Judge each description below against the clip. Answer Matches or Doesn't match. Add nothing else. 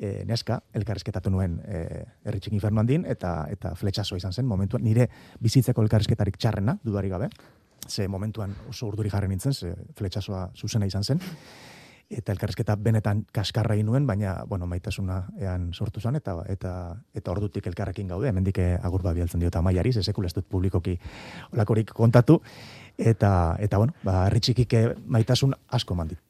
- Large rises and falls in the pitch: Doesn't match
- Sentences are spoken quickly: Doesn't match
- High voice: Doesn't match